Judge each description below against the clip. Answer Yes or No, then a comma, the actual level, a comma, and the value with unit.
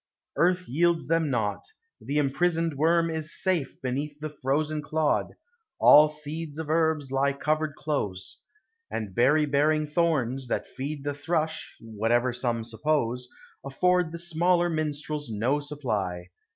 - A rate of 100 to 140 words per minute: Yes, slow, 135 wpm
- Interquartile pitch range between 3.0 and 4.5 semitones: Yes, average, 3.4 semitones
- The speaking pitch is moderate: Yes, medium, 150 Hz